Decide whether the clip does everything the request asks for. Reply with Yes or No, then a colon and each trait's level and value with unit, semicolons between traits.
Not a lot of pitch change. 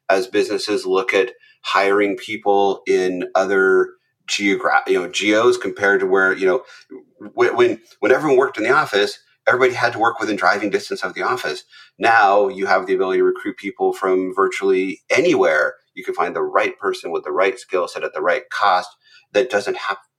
Yes: narrow, 1.8 semitones